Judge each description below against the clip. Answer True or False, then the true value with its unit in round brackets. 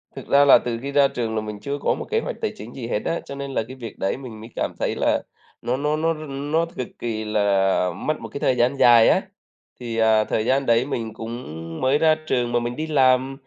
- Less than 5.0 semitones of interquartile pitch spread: True (3.7 semitones)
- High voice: False (125 Hz)